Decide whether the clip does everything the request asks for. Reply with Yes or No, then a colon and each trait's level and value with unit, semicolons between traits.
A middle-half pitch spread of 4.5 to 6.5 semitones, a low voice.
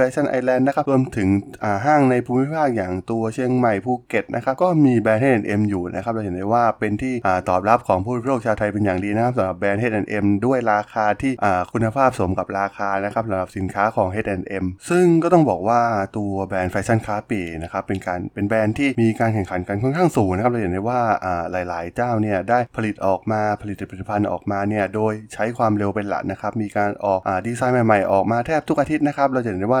No: average, 4.0 semitones; low, 105 Hz